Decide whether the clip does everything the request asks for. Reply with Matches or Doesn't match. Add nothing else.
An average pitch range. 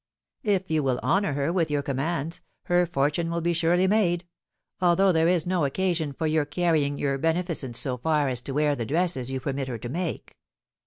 Matches